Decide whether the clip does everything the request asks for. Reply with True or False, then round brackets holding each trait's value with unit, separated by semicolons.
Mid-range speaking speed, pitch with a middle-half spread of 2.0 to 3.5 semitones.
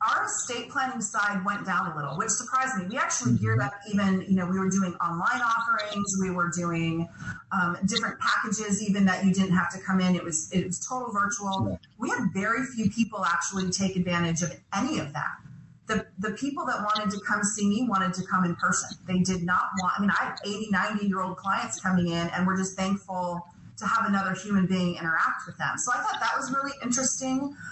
False (225 wpm; 2.8 semitones)